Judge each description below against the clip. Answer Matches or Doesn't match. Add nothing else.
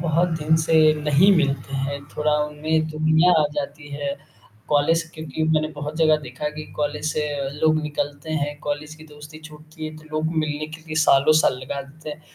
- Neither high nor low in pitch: Matches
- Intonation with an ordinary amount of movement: Doesn't match